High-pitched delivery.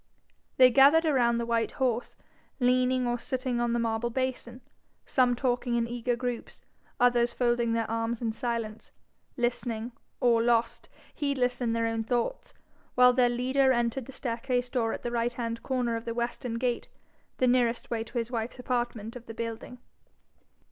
Yes: high, 240 Hz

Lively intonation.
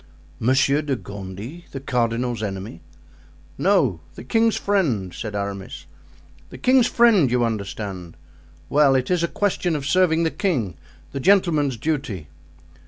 Yes: wide, 8.4 semitones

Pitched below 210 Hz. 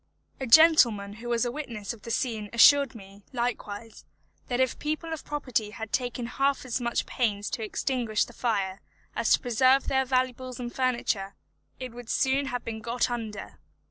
No: high, 240 Hz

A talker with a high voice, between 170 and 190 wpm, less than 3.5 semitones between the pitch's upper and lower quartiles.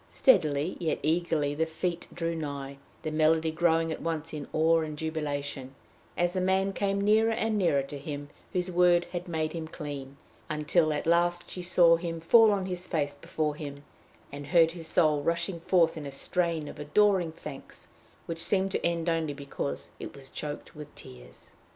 No: medium, 165 Hz; average, 180 wpm; average, 3.0 semitones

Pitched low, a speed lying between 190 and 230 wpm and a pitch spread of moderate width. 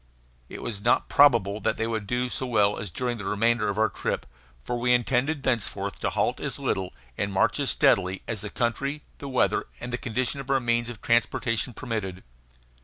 Yes: low, 115 Hz; average, 195 wpm; average, 3.0 semitones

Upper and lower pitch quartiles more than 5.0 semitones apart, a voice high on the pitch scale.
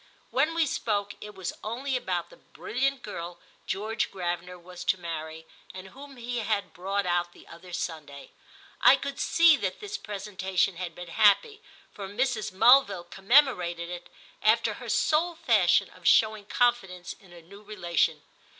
Yes: wide, 5.5 semitones; high, 200 Hz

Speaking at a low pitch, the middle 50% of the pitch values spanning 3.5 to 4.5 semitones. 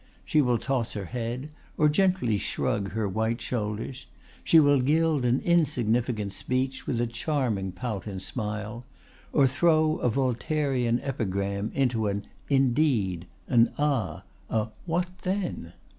No: low, 125 Hz; average, 5.0 semitones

